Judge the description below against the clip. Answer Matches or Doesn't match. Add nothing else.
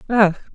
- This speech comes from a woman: Matches